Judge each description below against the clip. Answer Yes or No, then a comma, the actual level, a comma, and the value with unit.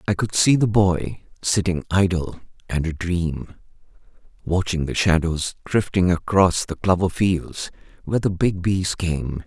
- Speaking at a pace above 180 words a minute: No, average, 145 wpm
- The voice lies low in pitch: Yes, very low, 90 Hz